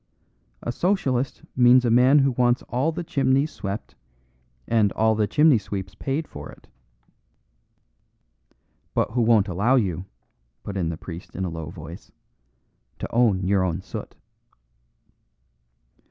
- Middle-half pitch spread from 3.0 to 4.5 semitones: No, wide, 5.6 semitones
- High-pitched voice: No, low, 115 Hz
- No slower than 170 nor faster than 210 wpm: No, average, 140 wpm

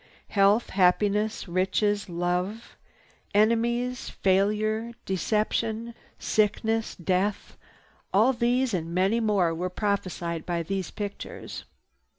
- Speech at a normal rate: No, slow, 90 wpm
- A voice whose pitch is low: No, high, 205 Hz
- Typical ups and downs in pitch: Yes, average, 3.3 semitones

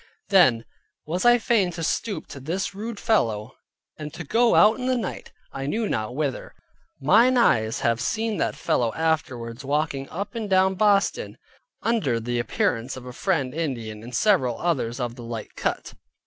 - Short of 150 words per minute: No, average, 175 wpm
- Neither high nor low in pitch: Yes, medium, 155 Hz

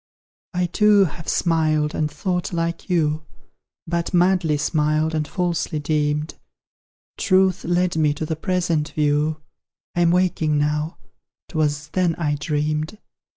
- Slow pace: Yes, slow, 125 wpm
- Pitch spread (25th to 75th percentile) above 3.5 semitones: No, narrow, 2.6 semitones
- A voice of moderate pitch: Yes, medium, 160 Hz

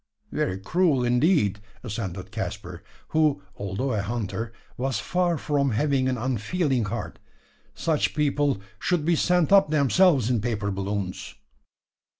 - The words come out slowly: Yes, slow, 130 wpm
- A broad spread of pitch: Yes, wide, 6.6 semitones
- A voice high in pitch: No, low, 130 Hz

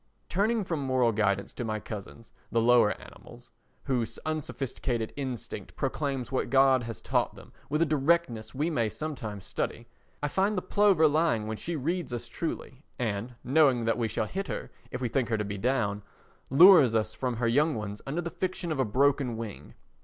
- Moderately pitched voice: No, low, 130 Hz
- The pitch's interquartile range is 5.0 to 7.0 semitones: Yes, average, 5.3 semitones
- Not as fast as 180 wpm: No, average, 185 wpm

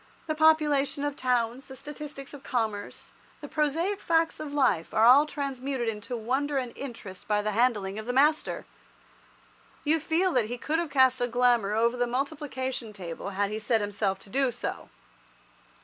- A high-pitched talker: Yes, very high, 255 Hz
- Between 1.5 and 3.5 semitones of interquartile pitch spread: No, average, 4.6 semitones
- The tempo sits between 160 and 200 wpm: Yes, average, 175 wpm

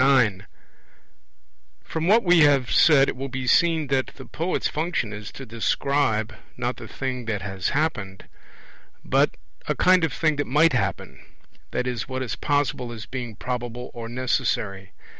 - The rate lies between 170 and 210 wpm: No, average, 160 wpm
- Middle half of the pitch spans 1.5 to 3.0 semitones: No, average, 4.3 semitones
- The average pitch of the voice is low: Yes, low, 130 Hz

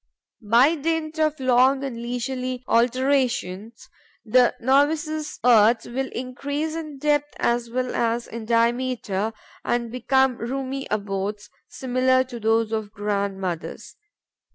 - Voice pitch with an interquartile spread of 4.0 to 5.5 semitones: No, average, 2.9 semitones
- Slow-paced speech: Yes, slow, 120 wpm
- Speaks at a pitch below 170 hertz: No, very high, 250 Hz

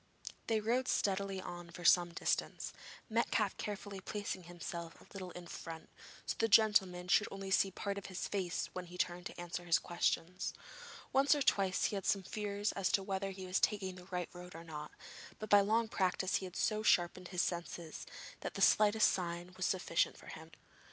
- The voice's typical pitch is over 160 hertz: Yes, medium, 185 Hz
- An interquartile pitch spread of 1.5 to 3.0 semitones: Yes, narrow, 2.5 semitones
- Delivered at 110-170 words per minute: No, average, 200 wpm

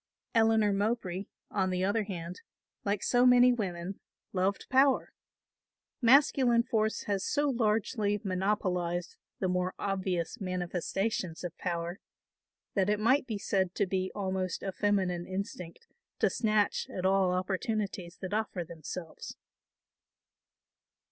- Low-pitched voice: No, high, 195 Hz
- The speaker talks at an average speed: No, slow, 120 wpm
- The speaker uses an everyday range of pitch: Yes, average, 3.1 semitones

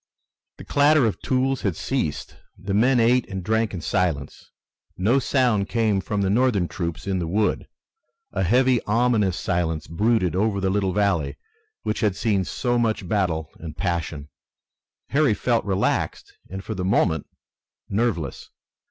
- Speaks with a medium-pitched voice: No, low, 100 Hz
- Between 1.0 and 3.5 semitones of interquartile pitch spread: No, average, 4.4 semitones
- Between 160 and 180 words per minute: No, average, 150 wpm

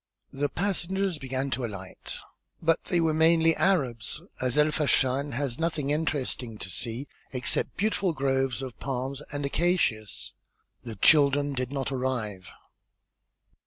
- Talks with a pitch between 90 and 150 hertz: Yes, medium, 140 Hz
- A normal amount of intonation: Yes, average, 4.0 semitones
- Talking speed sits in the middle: No, slow, 130 wpm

